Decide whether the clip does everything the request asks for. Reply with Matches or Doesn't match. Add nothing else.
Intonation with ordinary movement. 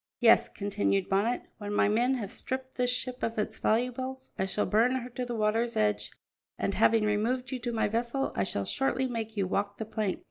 Matches